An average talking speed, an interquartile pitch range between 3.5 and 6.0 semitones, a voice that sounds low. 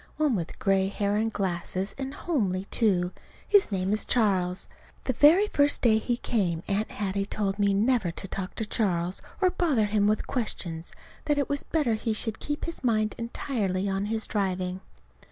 No: average, 180 wpm; average, 4.2 semitones; high, 210 Hz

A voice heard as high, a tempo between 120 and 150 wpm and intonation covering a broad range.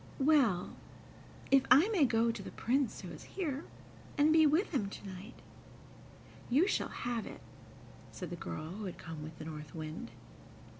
No: high, 235 Hz; average, 170 wpm; wide, 8.7 semitones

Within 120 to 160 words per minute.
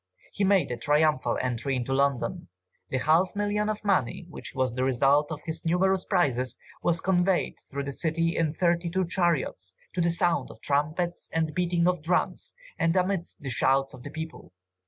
No: average, 180 wpm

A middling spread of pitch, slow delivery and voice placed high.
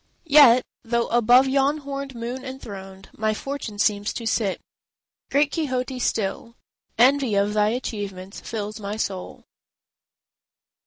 Yes: average, 4.3 semitones; slow, 110 wpm; high, 235 Hz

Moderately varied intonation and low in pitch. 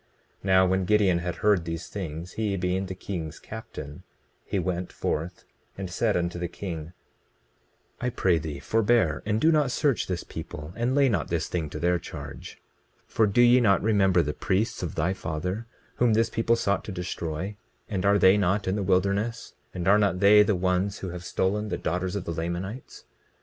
Yes: average, 3.3 semitones; very low, 95 Hz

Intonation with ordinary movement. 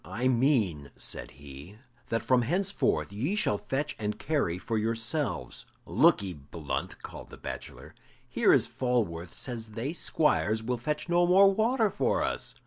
No: wide, 7.7 semitones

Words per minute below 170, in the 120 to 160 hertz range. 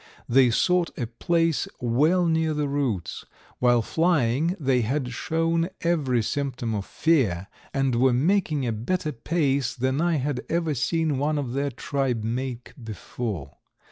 Yes: average, 145 wpm; low, 135 Hz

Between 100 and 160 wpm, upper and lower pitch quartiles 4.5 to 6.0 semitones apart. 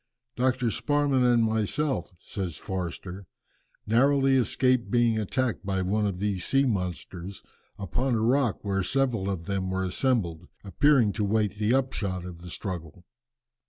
Yes: average, 145 wpm; average, 5.2 semitones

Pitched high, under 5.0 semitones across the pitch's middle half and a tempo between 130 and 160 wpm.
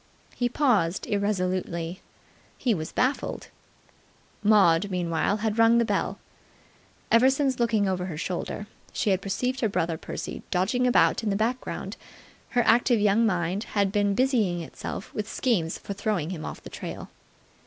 Yes: high, 205 Hz; average, 4.3 semitones; average, 155 wpm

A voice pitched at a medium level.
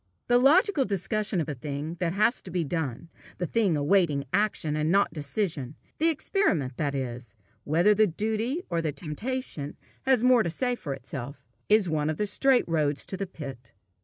Yes: medium, 175 Hz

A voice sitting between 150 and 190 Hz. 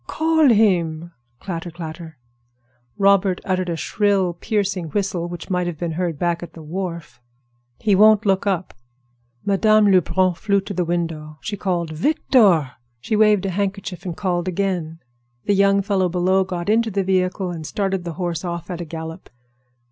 Yes: medium, 185 Hz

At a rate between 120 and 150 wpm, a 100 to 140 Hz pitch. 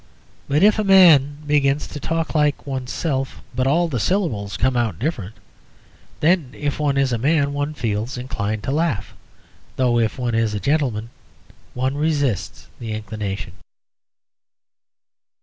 Yes: average, 145 wpm; low, 135 Hz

